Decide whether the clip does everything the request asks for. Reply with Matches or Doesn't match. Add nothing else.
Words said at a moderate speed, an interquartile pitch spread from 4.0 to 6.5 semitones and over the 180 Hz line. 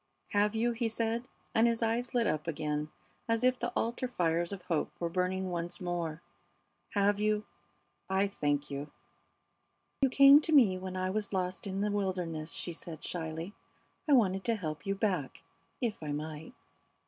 Matches